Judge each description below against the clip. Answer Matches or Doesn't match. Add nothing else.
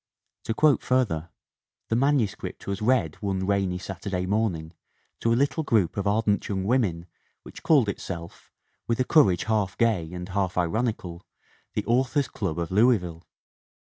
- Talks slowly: Doesn't match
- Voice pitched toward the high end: Doesn't match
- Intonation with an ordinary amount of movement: Matches